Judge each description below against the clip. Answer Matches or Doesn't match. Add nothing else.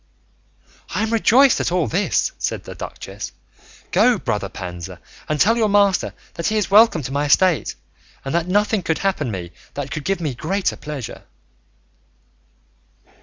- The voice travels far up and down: Matches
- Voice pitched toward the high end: Doesn't match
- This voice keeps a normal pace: Matches